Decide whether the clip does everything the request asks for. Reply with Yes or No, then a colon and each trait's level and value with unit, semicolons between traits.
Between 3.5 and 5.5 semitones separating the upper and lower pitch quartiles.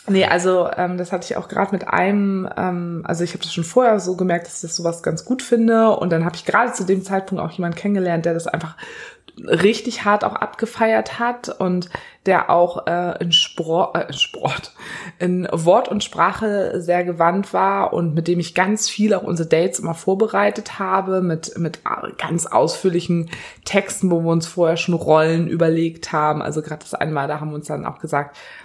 No: average, 2.8 semitones